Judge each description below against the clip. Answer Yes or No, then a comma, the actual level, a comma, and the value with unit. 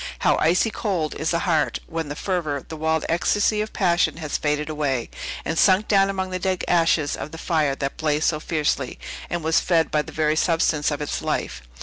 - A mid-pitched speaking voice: Yes, medium, 160 Hz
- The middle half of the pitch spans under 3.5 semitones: Yes, average, 2.9 semitones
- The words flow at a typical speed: No, fast, 210 wpm